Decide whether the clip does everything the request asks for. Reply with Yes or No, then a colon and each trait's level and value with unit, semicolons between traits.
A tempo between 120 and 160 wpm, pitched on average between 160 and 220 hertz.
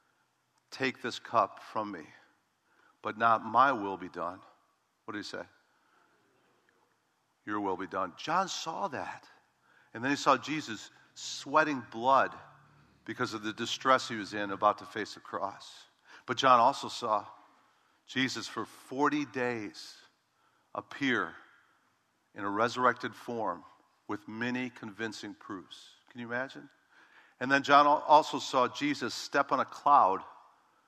No: average, 140 wpm; low, 125 Hz